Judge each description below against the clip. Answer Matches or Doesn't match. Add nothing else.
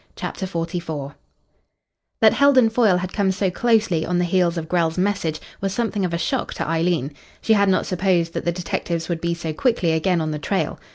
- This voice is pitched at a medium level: Matches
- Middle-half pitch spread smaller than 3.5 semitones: Matches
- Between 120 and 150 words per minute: Doesn't match